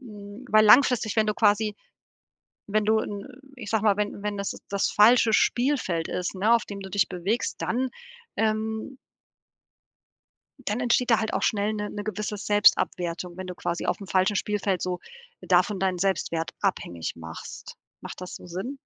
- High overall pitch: Yes, high, 205 Hz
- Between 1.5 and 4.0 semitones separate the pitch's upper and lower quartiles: Yes, average, 2.7 semitones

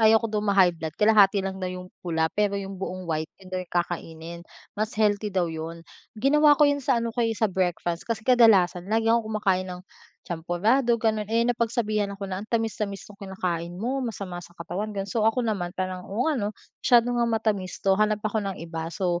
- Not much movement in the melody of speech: No, average, 3.7 semitones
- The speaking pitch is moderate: No, high, 200 Hz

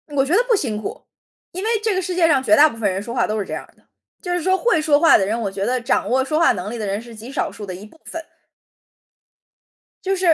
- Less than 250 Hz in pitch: No, very high, 265 Hz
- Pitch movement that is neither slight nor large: No, wide, 8.2 semitones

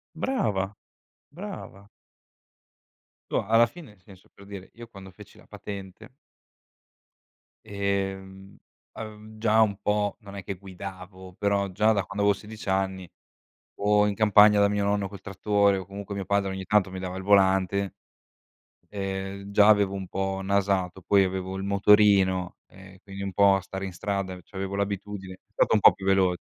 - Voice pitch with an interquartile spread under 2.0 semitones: Yes, narrow, 1.2 semitones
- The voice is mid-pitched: No, low, 100 Hz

